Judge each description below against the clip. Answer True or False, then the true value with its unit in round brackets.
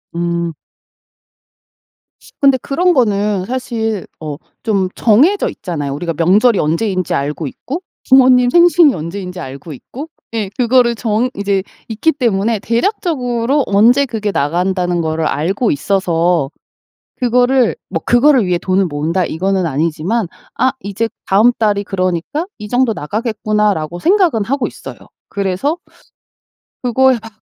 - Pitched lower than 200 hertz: False (210 Hz)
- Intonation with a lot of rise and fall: True (5.9 semitones)